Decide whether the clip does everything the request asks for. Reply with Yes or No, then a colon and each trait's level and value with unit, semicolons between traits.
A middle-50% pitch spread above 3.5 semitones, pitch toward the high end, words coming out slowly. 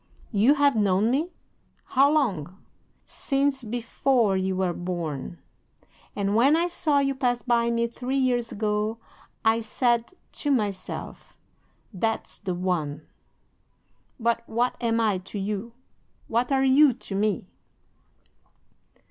Yes: average, 5.0 semitones; high, 230 Hz; slow, 125 wpm